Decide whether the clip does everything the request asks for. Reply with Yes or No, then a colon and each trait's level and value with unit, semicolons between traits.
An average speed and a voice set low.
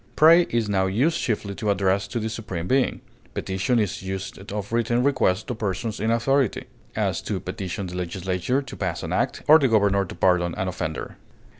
Yes: average, 190 wpm; low, 100 Hz